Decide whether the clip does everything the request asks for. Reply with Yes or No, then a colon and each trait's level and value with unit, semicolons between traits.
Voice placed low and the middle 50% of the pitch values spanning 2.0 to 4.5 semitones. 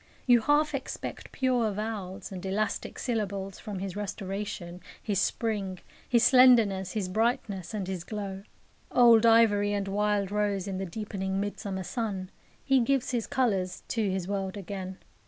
No: high, 205 Hz; average, 2.9 semitones